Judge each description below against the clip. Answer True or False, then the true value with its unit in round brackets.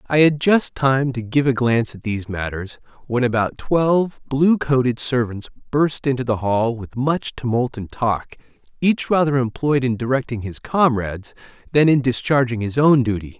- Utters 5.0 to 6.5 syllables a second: False (4.8 syllables/s)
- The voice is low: True (125 Hz)